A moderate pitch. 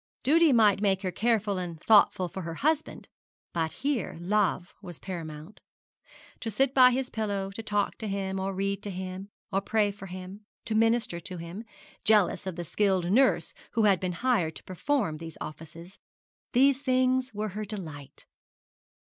No: high, 200 Hz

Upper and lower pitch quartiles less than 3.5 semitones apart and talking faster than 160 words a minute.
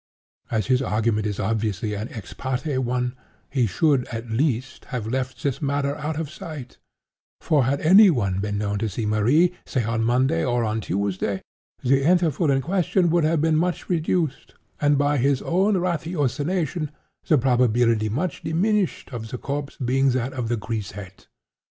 No: wide, 5.5 semitones; average, 170 wpm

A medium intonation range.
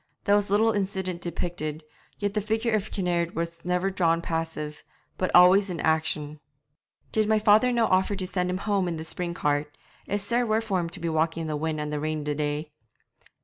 Yes: average, 4.2 semitones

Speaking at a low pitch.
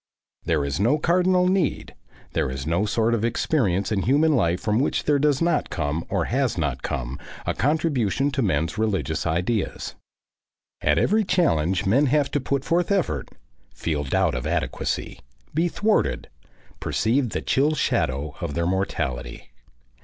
Yes: low, 115 Hz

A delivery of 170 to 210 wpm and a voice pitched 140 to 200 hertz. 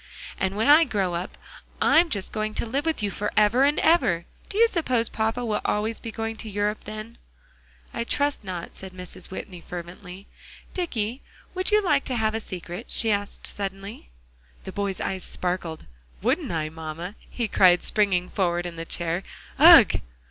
No: average, 175 wpm; high, 210 Hz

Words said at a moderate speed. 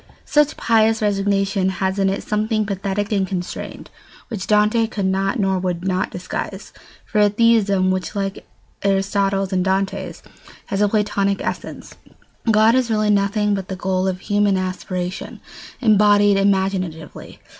Yes: average, 145 wpm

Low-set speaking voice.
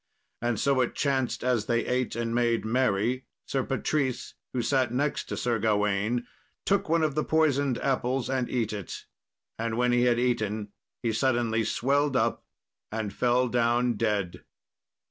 Yes: low, 120 Hz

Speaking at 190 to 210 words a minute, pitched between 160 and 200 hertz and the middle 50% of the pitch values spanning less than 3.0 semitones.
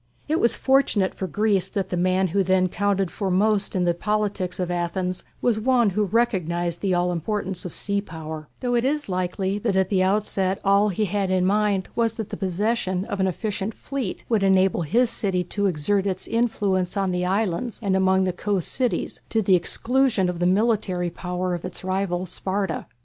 Yes: average, 200 wpm; high, 190 Hz; narrow, 2.6 semitones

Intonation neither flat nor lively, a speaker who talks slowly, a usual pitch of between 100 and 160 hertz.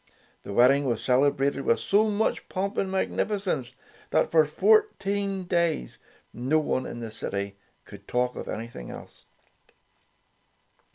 No: wide, 8.3 semitones; slow, 130 wpm; medium, 140 Hz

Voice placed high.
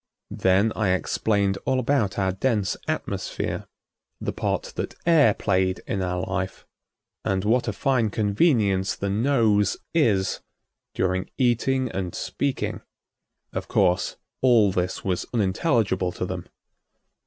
No: low, 100 Hz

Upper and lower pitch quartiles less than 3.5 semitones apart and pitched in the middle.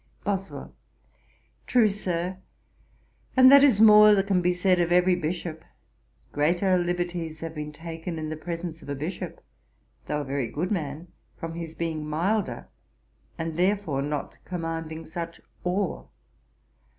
Yes: average, 2.8 semitones; medium, 170 Hz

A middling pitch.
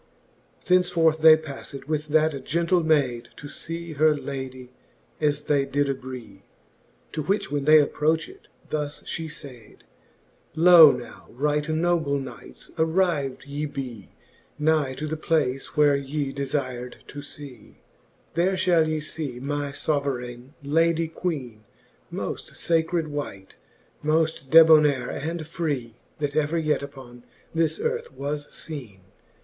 Yes: medium, 150 Hz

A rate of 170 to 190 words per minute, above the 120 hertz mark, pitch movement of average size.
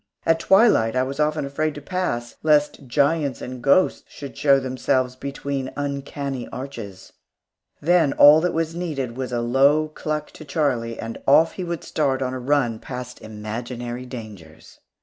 No: average, 160 wpm; low, 135 Hz; average, 3.5 semitones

